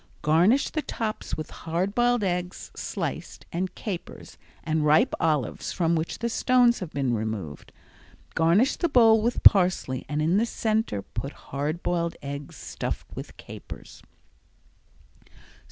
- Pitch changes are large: Yes, wide, 6.5 semitones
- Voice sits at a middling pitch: Yes, medium, 175 Hz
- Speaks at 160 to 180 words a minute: No, slow, 135 wpm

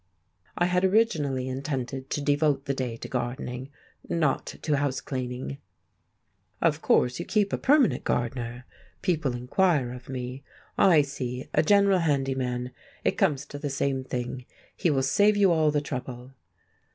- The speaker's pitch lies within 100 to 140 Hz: Yes, low, 135 Hz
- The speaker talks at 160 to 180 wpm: No, average, 150 wpm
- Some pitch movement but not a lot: Yes, average, 3.7 semitones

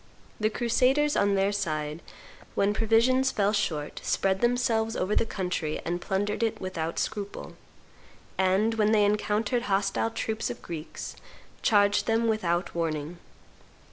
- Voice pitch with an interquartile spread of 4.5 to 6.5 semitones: No, average, 3.3 semitones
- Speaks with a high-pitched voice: Yes, high, 205 Hz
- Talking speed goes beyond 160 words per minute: No, slow, 135 wpm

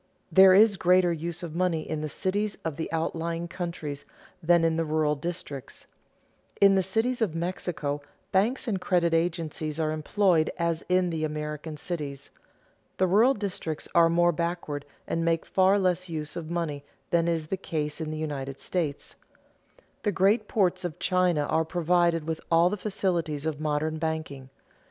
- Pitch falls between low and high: Yes, medium, 165 Hz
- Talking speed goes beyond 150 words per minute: Yes, average, 165 wpm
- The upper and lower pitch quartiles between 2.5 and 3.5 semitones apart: Yes, average, 2.8 semitones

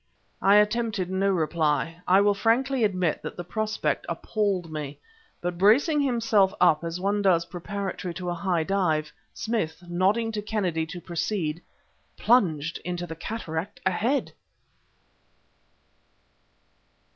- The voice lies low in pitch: No, medium, 185 Hz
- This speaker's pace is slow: Yes, slow, 125 wpm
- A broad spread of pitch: No, average, 4.0 semitones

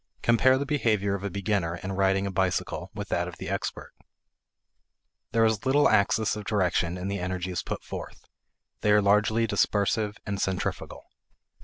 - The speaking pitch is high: No, low, 100 Hz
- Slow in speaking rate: No, average, 165 wpm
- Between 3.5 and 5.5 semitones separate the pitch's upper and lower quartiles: No, narrow, 2.4 semitones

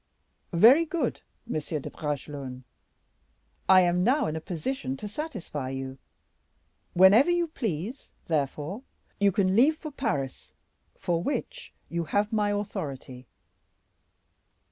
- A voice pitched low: No, medium, 185 Hz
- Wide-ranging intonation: Yes, wide, 8.2 semitones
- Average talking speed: No, slow, 120 wpm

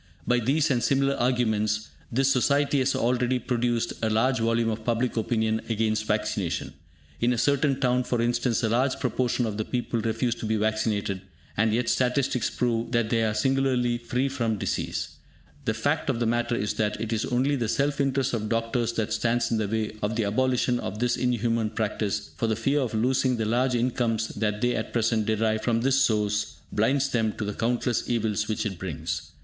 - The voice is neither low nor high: No, low, 115 Hz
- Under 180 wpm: No, average, 200 wpm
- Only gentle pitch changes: Yes, narrow, 2.3 semitones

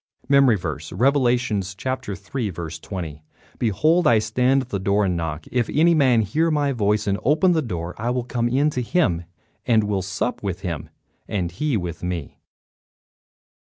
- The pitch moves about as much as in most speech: No, wide, 6.5 semitones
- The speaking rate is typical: Yes, average, 165 wpm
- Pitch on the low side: Yes, low, 110 Hz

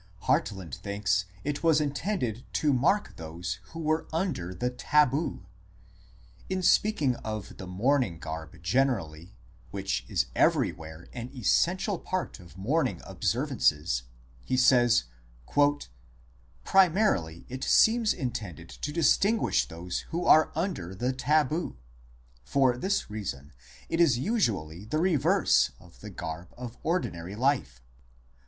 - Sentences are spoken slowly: Yes, slow, 125 wpm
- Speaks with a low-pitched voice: Yes, low, 120 Hz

